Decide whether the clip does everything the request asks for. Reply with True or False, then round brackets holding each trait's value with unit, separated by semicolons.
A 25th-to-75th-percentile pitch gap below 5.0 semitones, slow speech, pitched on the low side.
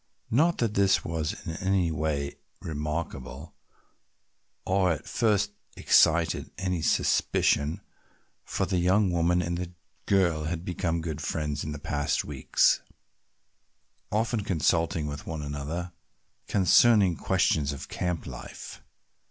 True (3.6 semitones; 120 wpm; 85 Hz)